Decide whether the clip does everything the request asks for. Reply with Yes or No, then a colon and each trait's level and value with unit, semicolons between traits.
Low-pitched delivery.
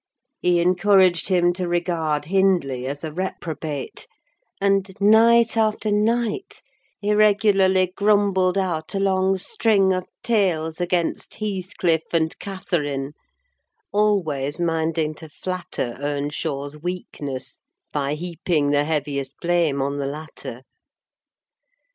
No: medium, 175 Hz